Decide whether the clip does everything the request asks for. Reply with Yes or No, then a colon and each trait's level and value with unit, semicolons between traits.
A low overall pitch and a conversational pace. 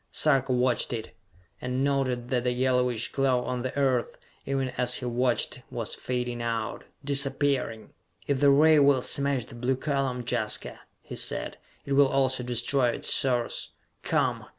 Yes: low, 130 Hz; average, 155 wpm